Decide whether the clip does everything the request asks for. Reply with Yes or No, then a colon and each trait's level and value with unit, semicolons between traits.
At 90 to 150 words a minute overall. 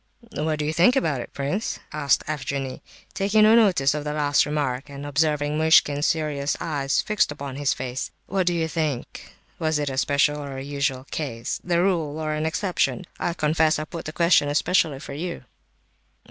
No: average, 180 wpm